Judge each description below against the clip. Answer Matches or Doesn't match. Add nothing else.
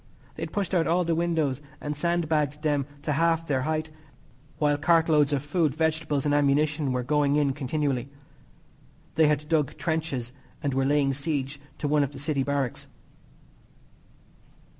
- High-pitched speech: Doesn't match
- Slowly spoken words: Doesn't match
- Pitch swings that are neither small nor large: Doesn't match